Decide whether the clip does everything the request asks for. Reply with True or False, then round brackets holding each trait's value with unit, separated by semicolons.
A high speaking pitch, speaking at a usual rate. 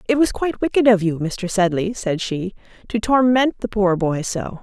False (210 Hz; 210 wpm)